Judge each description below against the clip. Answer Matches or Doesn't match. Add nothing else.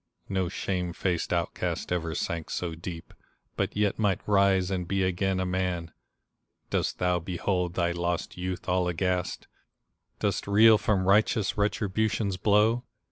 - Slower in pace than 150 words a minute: Matches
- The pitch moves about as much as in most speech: Doesn't match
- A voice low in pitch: Matches